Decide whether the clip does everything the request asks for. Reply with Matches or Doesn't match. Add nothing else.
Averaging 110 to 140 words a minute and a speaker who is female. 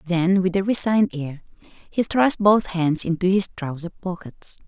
Doesn't match